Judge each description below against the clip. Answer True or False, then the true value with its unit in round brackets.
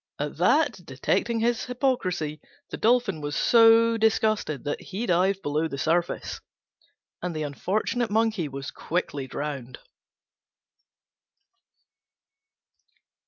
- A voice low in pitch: False (185 Hz)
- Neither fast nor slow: False (105 wpm)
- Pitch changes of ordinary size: False (7.1 semitones)